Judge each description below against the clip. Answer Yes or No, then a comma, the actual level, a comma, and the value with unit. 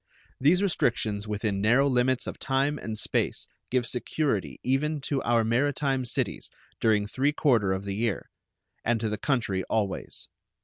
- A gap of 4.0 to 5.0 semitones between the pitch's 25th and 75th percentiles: Yes, average, 4.3 semitones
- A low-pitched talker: Yes, low, 120 Hz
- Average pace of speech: Yes, average, 150 wpm